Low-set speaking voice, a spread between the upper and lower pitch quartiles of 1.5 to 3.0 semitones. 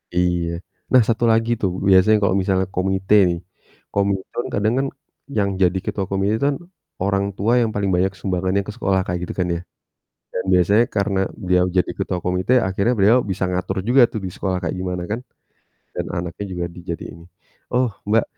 Yes: very low, 95 Hz; narrow, 2.6 semitones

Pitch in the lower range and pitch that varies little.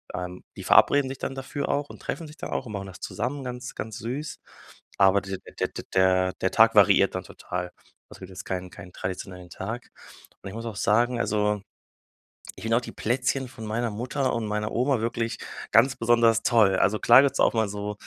No: low, 115 Hz; average, 4.1 semitones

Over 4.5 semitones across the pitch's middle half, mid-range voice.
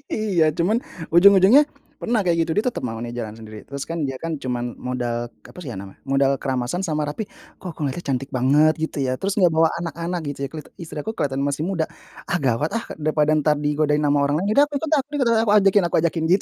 Yes: average, 5.1 semitones; medium, 155 Hz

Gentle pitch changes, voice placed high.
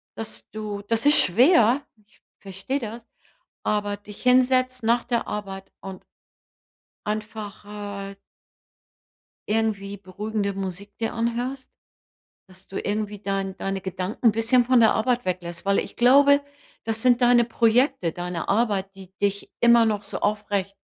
No: average, 3.2 semitones; high, 210 Hz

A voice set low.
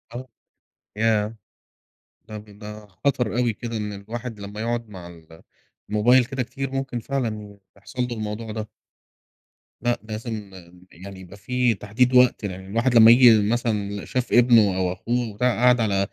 Yes: low, 110 Hz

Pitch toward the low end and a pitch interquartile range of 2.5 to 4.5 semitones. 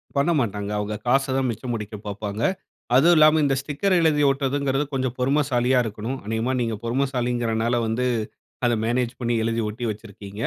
Yes: low, 125 Hz; average, 3.3 semitones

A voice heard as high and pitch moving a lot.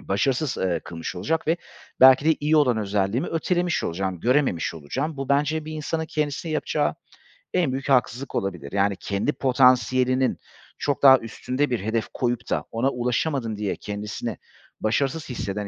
No: low, 125 Hz; wide, 5.8 semitones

